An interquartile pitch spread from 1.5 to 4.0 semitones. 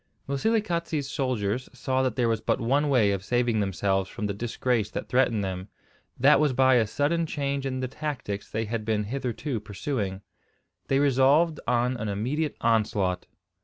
No: average, 4.6 semitones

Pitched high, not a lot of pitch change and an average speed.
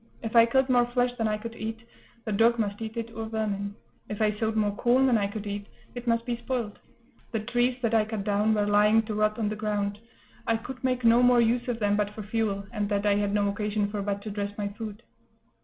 No: high, 220 Hz; narrow, 2.1 semitones; fast, 250 wpm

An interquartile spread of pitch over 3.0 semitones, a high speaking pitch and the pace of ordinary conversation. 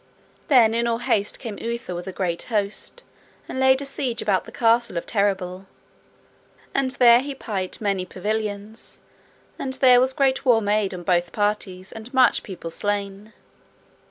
Yes: average, 4.1 semitones; high, 215 Hz; average, 160 wpm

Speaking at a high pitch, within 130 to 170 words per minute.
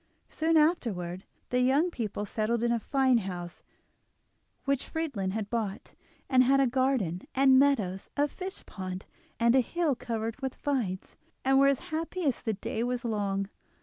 Yes: high, 245 Hz; average, 160 wpm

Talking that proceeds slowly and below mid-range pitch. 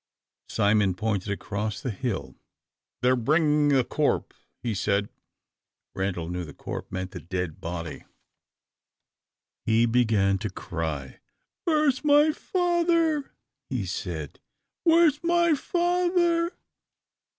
Yes: slow, 115 wpm; low, 120 Hz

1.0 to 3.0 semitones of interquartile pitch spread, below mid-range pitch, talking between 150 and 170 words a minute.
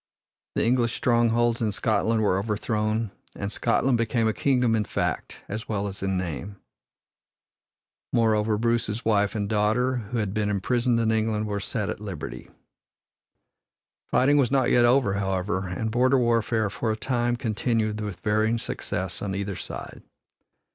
Yes: narrow, 2.4 semitones; low, 110 Hz; average, 155 wpm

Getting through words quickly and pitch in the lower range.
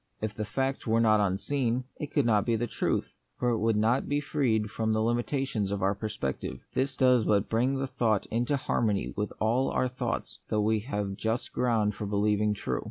Yes: fast, 210 wpm; low, 110 Hz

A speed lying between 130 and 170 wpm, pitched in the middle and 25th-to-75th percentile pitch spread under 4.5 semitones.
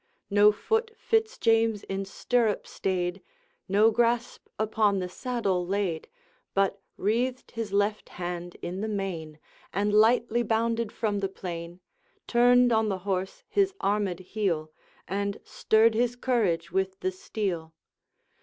No: slow, 135 wpm; high, 205 Hz; average, 3.5 semitones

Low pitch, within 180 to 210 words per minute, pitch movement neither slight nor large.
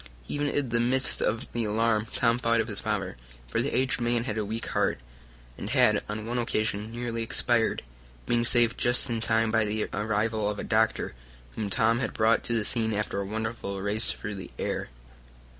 No: low, 110 Hz; average, 195 wpm; narrow, 1.7 semitones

